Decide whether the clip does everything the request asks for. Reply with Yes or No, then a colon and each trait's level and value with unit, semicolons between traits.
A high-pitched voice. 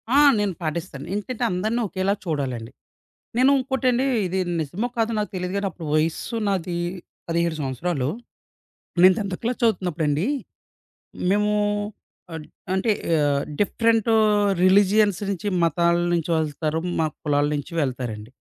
No: medium, 180 Hz